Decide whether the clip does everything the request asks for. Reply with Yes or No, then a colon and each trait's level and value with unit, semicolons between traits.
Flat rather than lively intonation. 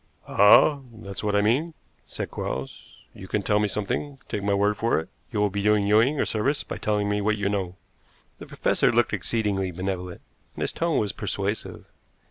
Yes: narrow, 1.6 semitones